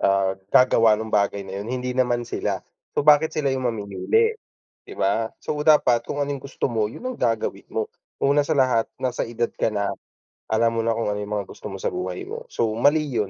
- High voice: No, low, 120 Hz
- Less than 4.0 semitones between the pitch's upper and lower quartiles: No, average, 4.7 semitones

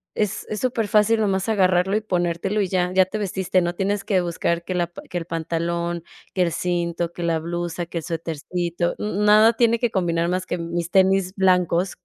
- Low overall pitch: No, medium, 180 Hz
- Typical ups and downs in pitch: No, narrow, 2.3 semitones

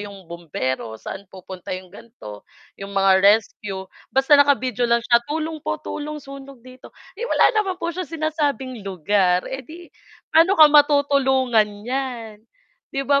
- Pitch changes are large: Yes, wide, 6.7 semitones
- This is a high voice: Yes, very high, 255 Hz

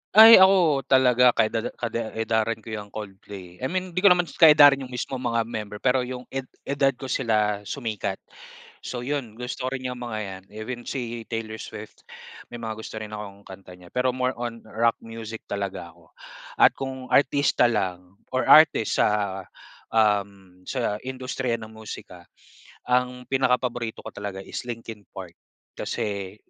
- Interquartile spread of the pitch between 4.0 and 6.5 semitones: No, average, 3.6 semitones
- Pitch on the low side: Yes, low, 115 Hz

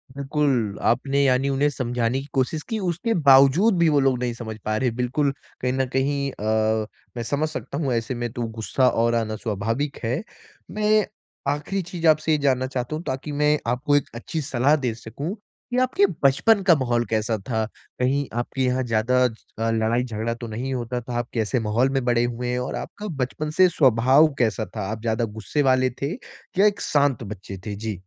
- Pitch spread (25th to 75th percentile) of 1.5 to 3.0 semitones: No, average, 3.7 semitones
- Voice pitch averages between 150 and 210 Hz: No, low, 130 Hz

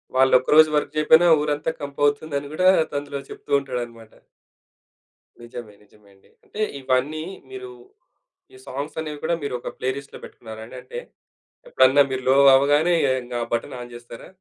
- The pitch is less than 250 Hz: Yes, medium, 140 Hz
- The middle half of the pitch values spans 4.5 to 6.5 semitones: No, average, 3.6 semitones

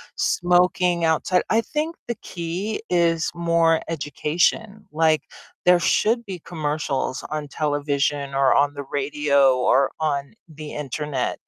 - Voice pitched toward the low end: No, medium, 155 Hz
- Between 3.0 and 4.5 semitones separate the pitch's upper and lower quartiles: Yes, average, 3.6 semitones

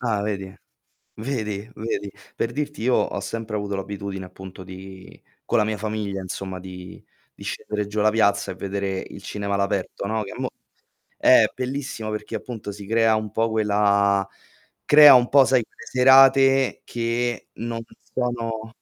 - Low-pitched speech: Yes, low, 105 Hz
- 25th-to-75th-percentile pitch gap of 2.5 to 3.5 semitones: Yes, average, 2.9 semitones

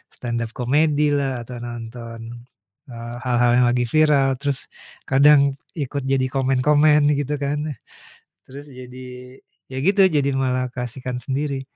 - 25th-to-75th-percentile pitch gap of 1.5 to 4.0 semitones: Yes, narrow, 2.6 semitones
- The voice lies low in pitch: Yes, low, 130 Hz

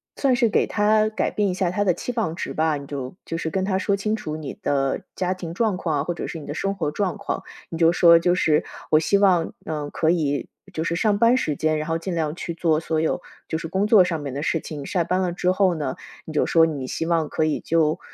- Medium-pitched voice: Yes, medium, 170 Hz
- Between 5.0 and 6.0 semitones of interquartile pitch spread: No, average, 3.5 semitones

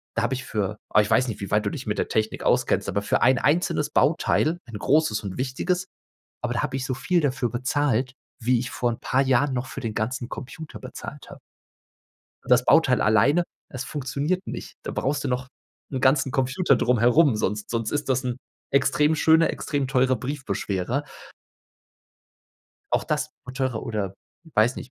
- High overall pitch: No, low, 130 Hz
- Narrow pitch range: No, average, 3.5 semitones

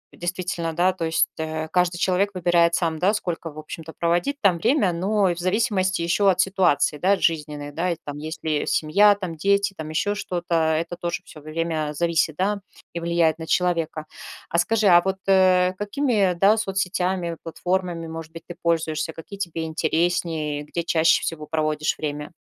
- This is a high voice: No, medium, 170 Hz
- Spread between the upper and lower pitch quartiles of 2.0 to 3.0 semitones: Yes, narrow, 2.6 semitones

